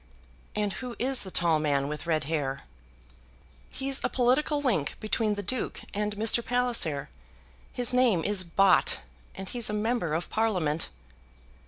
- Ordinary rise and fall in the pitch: No, wide, 7.0 semitones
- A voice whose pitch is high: Yes, high, 210 Hz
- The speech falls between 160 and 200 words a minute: No, average, 150 wpm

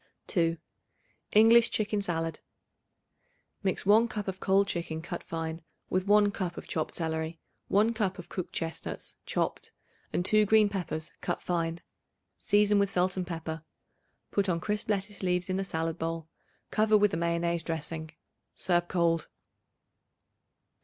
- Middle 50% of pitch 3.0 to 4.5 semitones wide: Yes, average, 3.7 semitones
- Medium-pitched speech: Yes, medium, 180 Hz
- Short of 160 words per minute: Yes, average, 145 wpm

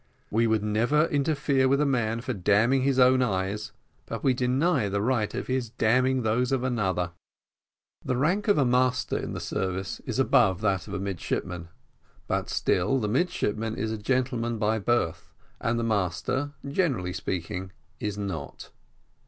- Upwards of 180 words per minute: No, average, 165 wpm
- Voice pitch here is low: Yes, low, 115 Hz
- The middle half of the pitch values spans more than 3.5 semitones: Yes, average, 4.4 semitones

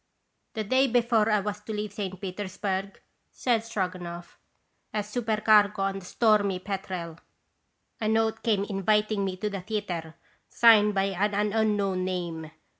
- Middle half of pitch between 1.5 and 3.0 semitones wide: Yes, narrow, 2.4 semitones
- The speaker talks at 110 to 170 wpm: Yes, average, 150 wpm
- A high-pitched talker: Yes, high, 205 Hz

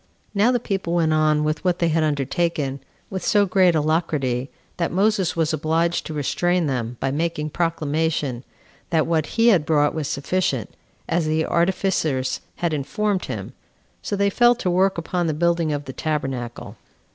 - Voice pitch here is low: No, medium, 160 Hz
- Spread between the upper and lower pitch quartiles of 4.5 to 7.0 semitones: No, average, 3.2 semitones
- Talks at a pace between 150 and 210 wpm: Yes, average, 170 wpm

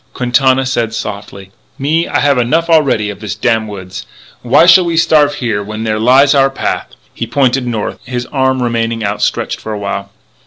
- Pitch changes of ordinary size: Yes, average, 4.2 semitones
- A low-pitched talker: Yes, low, 120 Hz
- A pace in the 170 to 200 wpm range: Yes, average, 185 wpm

